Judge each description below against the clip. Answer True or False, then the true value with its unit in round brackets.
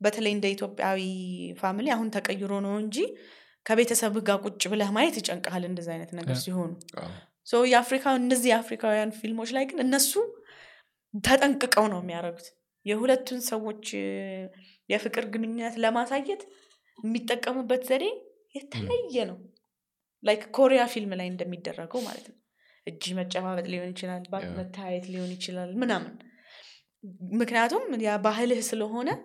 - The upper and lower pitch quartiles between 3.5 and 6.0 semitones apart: True (5.0 semitones)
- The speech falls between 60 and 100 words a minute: False (110 wpm)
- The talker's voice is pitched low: False (220 Hz)